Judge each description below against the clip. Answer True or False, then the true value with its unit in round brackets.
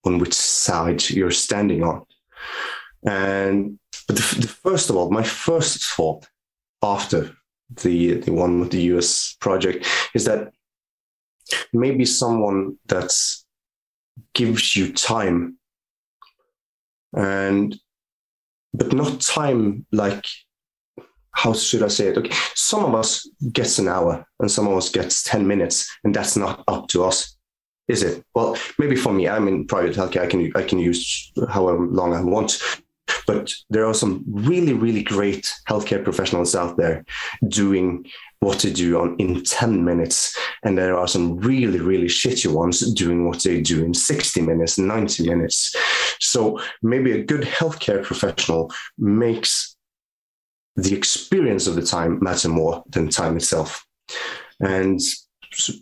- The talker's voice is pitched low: True (95 Hz)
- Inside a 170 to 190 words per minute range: False (145 wpm)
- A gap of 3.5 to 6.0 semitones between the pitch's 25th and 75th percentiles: True (3.9 semitones)